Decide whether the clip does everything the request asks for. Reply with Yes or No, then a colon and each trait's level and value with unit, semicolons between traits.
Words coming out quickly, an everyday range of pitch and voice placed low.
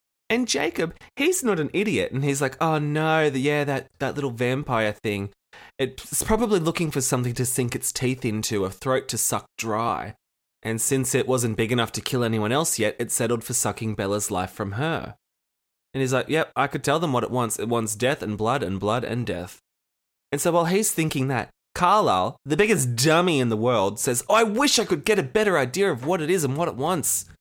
No: fast, 225 wpm; wide, 5.9 semitones; low, 130 Hz